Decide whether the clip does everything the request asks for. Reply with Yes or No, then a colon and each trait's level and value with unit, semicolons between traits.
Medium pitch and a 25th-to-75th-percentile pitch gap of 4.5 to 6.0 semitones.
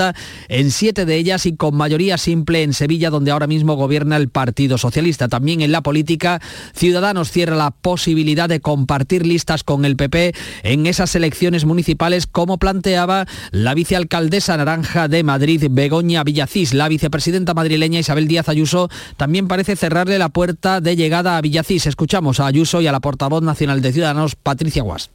No: medium, 160 Hz; average, 2.9 semitones